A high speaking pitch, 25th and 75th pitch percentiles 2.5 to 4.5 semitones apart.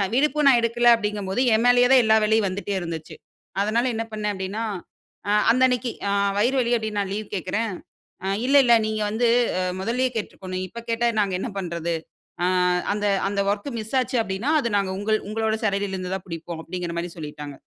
Yes: high, 215 Hz; average, 3.7 semitones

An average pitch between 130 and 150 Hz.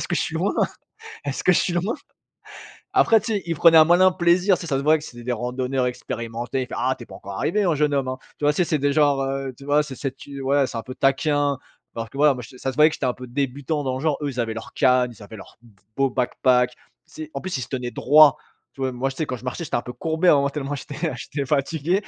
Yes: medium, 140 Hz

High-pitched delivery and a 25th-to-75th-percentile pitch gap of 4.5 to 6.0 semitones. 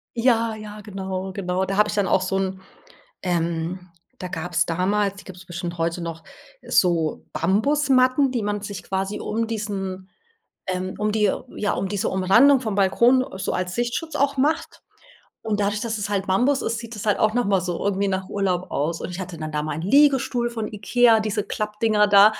No: high, 200 Hz; average, 3.3 semitones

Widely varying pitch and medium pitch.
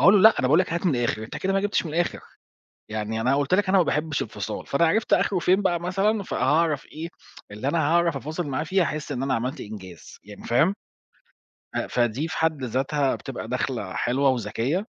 Yes: wide, 5.7 semitones; medium, 150 Hz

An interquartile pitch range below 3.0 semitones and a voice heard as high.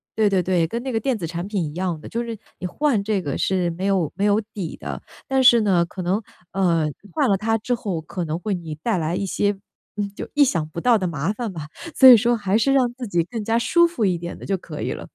No: average, 5.0 semitones; high, 195 Hz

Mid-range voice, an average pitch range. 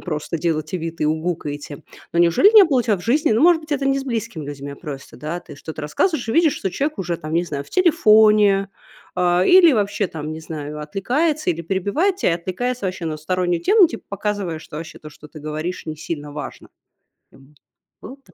No: medium, 180 Hz; wide, 7.9 semitones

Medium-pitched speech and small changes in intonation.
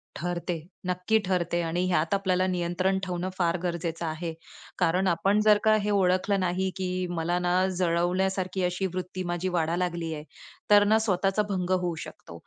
Yes: medium, 180 Hz; narrow, 1.6 semitones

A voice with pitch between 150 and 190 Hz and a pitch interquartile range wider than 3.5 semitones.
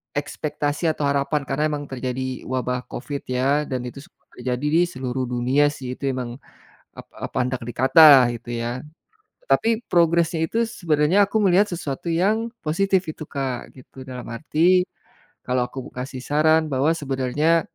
No: medium, 140 Hz; average, 4.0 semitones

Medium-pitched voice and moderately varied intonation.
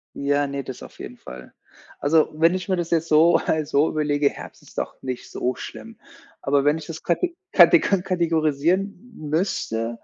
Yes: medium, 155 Hz; average, 3.2 semitones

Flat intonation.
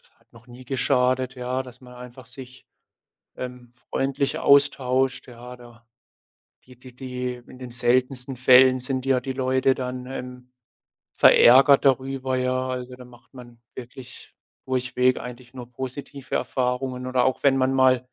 Yes: narrow, 0.8 semitones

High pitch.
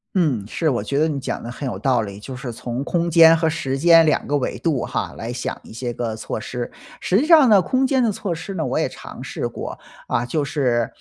No: medium, 140 Hz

